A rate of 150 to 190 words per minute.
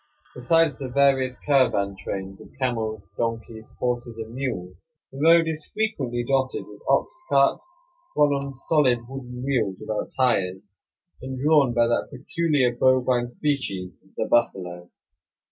No: slow, 135 wpm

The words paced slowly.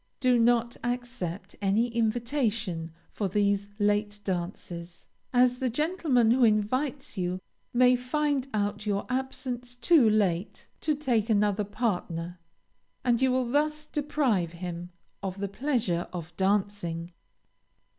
Yes: slow, 125 wpm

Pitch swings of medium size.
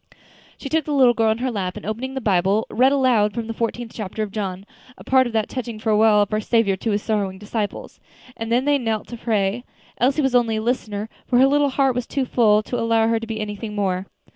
Yes: average, 3.0 semitones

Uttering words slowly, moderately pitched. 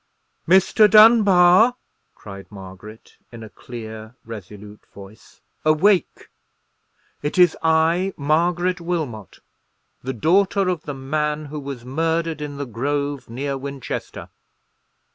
Yes: slow, 110 wpm; medium, 145 Hz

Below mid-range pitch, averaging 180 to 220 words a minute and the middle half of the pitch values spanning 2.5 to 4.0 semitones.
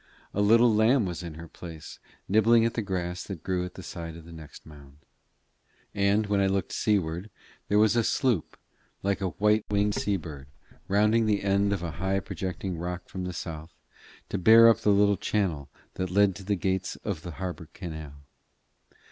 Yes: very low, 95 Hz; average, 190 wpm; average, 3.4 semitones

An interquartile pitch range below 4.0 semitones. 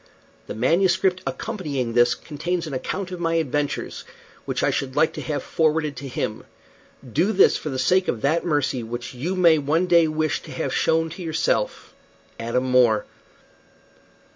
No: average, 4.6 semitones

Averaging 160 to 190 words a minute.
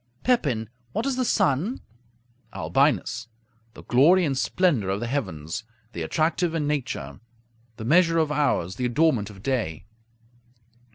No: slow, 135 wpm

